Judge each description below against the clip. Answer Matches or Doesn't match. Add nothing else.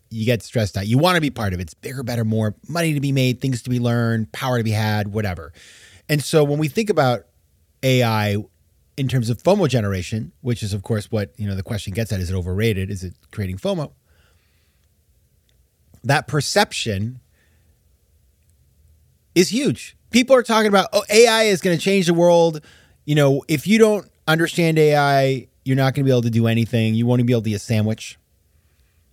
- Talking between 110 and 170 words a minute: Doesn't match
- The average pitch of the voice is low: Matches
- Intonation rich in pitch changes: Matches